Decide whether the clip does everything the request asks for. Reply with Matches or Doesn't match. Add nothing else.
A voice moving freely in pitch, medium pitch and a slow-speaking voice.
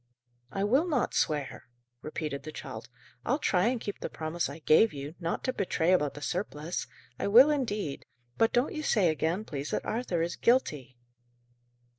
Doesn't match